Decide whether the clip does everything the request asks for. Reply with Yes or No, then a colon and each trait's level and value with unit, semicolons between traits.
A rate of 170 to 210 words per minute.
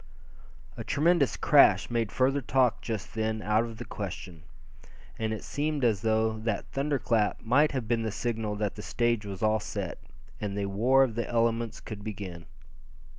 Yes: average, 175 wpm